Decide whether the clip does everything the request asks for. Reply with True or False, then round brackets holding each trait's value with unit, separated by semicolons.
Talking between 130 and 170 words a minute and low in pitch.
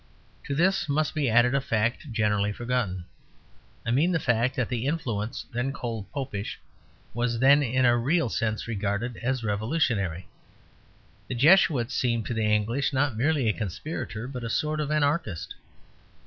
True (160 wpm; 120 Hz)